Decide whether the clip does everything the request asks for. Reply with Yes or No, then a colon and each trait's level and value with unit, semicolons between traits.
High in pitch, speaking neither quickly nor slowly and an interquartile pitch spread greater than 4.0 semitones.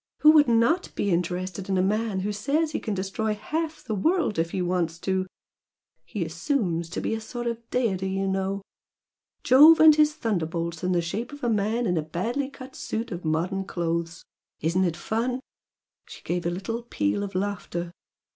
Yes: high, 195 Hz; average, 190 wpm; wide, 5.4 semitones